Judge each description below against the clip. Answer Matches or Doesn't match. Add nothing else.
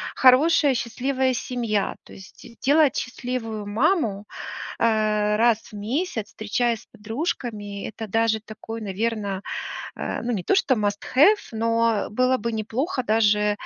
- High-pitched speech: Matches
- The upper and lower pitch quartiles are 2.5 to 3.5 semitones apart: Matches